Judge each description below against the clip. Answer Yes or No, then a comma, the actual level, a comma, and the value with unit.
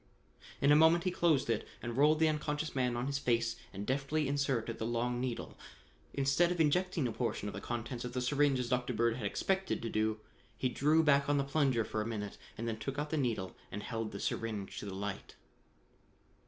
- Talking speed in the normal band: No, fast, 220 wpm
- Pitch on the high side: No, low, 125 Hz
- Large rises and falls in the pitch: No, average, 4.3 semitones